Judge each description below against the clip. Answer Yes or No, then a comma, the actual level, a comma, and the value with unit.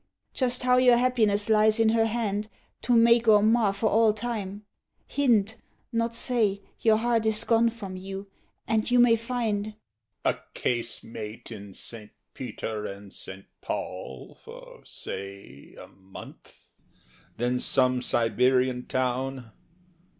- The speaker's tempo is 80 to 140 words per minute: Yes, slow, 135 wpm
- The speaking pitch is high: Yes, high, 210 Hz